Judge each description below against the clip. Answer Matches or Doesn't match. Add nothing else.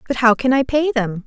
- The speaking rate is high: Matches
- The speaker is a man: Doesn't match